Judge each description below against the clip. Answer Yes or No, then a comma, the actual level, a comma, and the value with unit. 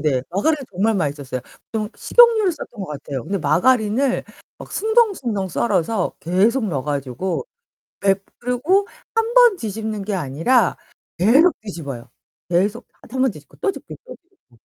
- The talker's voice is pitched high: Yes, high, 205 Hz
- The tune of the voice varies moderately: No, wide, 8.2 semitones